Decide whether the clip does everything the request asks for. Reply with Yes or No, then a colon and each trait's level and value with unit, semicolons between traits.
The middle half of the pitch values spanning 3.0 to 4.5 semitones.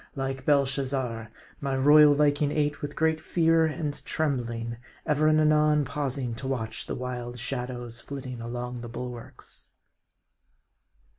Yes: average, 3.3 semitones